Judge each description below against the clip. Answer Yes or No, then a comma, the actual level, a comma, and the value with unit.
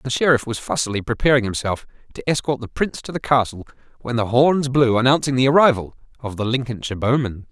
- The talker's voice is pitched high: No, low, 125 Hz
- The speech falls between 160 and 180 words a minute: No, average, 190 wpm